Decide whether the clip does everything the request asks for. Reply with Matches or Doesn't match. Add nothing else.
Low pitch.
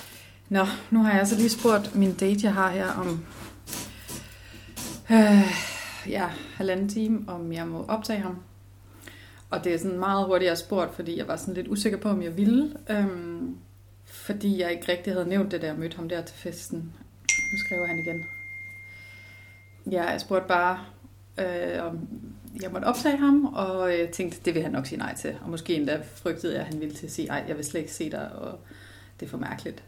Doesn't match